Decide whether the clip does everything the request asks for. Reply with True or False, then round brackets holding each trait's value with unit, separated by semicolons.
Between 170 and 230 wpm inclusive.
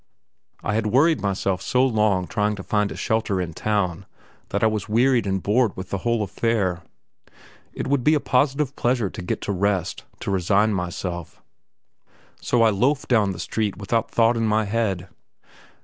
True (180 wpm)